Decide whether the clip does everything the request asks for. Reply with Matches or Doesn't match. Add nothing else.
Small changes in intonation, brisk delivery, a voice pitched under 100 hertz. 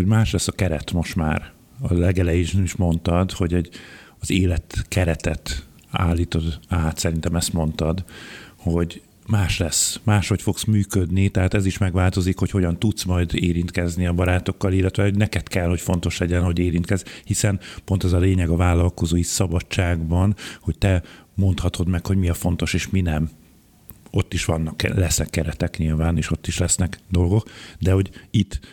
Matches